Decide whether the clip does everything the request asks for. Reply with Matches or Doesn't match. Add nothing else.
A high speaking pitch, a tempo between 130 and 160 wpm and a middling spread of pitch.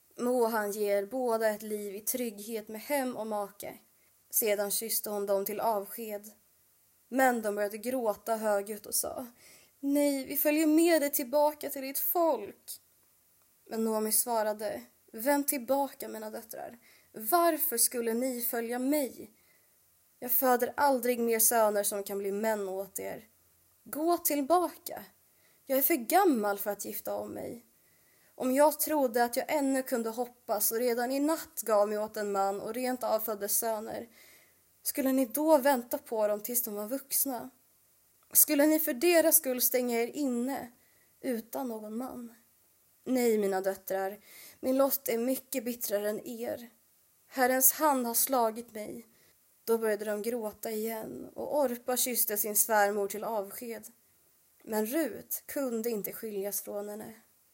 Matches